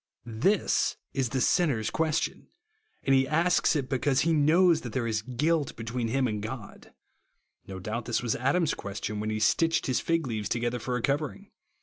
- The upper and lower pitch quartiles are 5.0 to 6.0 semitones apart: Yes, wide, 5.6 semitones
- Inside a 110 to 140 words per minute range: No, average, 190 wpm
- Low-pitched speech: Yes, low, 130 Hz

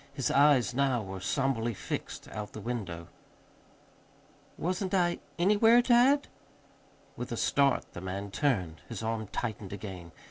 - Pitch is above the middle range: No, low, 120 Hz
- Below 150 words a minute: Yes, slow, 135 wpm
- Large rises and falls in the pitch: Yes, wide, 7.6 semitones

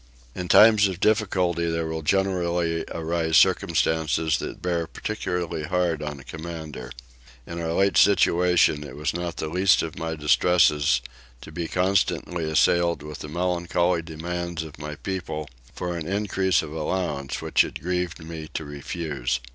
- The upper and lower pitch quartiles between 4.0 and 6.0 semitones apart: No, narrow, 2.4 semitones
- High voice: No, very low, 85 Hz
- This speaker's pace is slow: No, average, 155 wpm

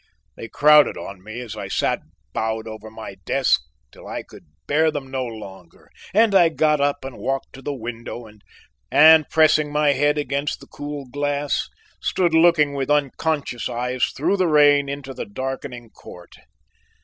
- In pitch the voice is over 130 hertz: Yes, medium, 140 Hz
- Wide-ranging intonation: No, average, 3.8 semitones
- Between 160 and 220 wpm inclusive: Yes, average, 165 wpm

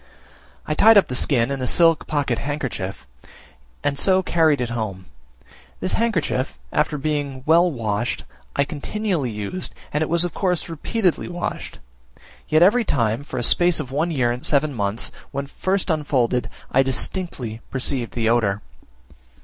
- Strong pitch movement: Yes, wide, 5.8 semitones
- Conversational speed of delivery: Yes, average, 160 wpm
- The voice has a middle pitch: Yes, medium, 145 Hz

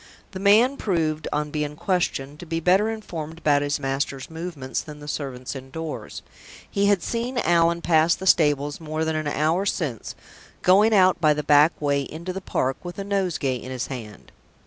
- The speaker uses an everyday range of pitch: Yes, average, 4.0 semitones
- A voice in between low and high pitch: Yes, medium, 160 Hz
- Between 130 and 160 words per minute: No, average, 185 wpm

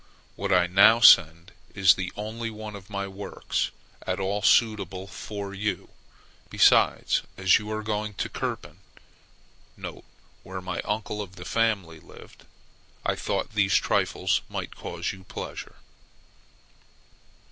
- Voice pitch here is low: Yes, low, 100 Hz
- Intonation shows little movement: Yes, narrow, 2.3 semitones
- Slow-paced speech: Yes, slow, 130 wpm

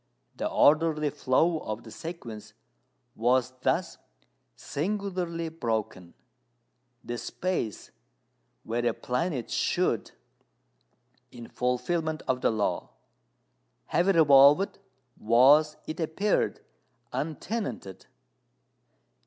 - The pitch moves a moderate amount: No, wide, 5.7 semitones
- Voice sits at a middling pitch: Yes, medium, 145 Hz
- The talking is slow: Yes, slow, 85 wpm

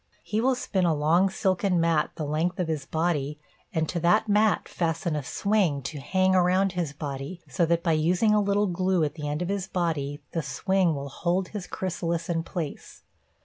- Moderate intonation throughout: Yes, average, 3.5 semitones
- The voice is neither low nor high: Yes, medium, 170 Hz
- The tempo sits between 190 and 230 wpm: Yes, average, 200 wpm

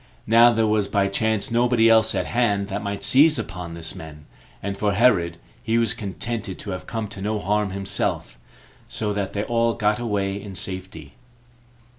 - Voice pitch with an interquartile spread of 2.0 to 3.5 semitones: Yes, narrow, 2.6 semitones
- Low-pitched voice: Yes, low, 105 Hz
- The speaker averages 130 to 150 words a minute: No, average, 180 wpm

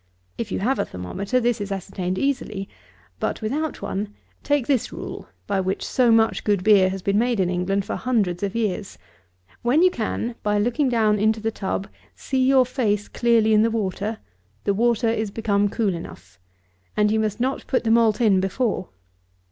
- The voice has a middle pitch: No, high, 215 Hz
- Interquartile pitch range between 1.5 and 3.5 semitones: Yes, average, 3.2 semitones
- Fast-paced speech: No, average, 190 wpm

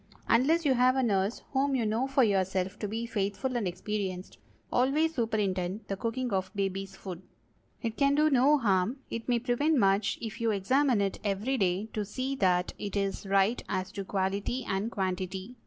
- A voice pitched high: Yes, high, 210 Hz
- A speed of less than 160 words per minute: No, average, 175 wpm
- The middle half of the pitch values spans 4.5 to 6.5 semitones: Yes, average, 4.8 semitones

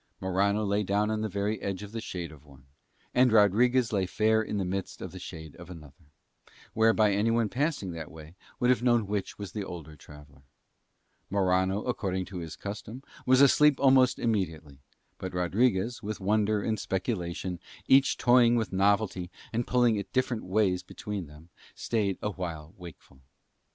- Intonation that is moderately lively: Yes, average, 3.8 semitones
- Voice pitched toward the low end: Yes, low, 100 Hz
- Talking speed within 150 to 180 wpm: Yes, average, 165 wpm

